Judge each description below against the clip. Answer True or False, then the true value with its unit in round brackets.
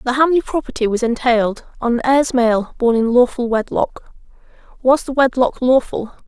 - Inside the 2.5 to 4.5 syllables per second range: False (4.9 syllables/s)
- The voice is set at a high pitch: True (250 Hz)